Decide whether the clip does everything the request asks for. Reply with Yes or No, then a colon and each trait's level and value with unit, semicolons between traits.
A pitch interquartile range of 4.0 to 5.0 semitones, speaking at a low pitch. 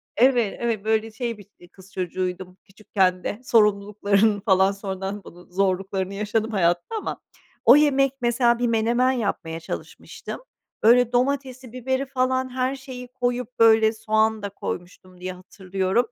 No: average, 4.4 semitones; high, 220 Hz